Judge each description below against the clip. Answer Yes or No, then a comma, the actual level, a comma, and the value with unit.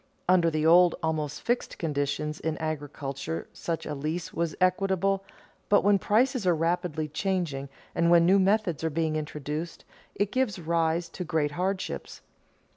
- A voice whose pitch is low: No, medium, 165 Hz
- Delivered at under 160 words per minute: Yes, average, 150 wpm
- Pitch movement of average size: Yes, average, 3.4 semitones